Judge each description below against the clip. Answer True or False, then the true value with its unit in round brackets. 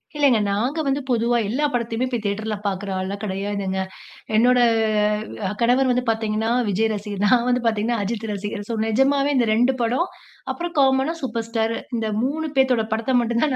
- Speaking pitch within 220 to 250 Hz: True (230 Hz)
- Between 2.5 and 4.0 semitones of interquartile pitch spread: True (3.3 semitones)